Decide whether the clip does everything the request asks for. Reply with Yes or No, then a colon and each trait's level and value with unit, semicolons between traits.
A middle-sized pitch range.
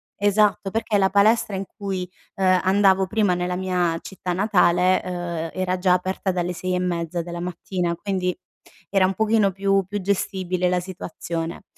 No: narrow, 1.7 semitones